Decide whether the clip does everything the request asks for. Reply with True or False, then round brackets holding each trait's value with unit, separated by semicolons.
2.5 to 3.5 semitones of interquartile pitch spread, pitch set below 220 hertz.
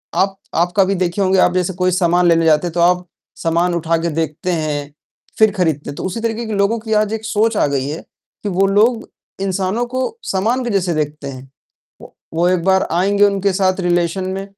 True (3.1 semitones; 185 Hz)